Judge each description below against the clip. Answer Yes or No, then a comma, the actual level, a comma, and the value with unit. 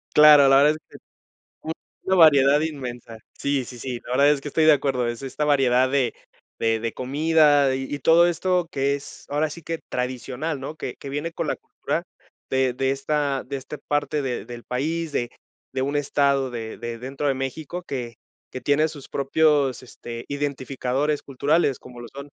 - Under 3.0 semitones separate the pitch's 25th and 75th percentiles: Yes, narrow, 2.6 semitones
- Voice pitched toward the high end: No, medium, 140 Hz